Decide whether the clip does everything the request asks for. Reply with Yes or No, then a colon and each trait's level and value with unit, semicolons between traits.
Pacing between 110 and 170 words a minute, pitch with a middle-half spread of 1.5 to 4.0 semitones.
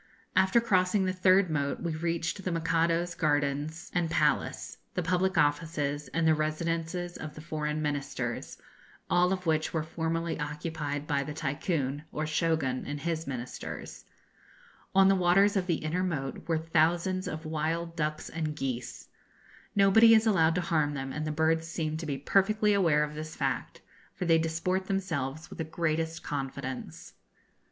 Yes: average, 160 wpm; average, 2.7 semitones